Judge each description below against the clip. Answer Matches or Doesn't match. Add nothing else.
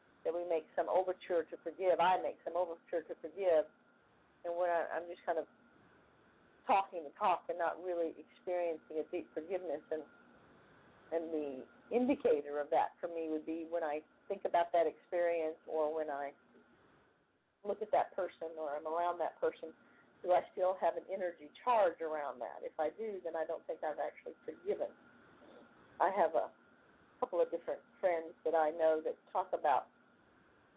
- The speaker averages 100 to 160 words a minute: Doesn't match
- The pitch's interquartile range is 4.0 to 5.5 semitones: Doesn't match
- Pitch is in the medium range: Matches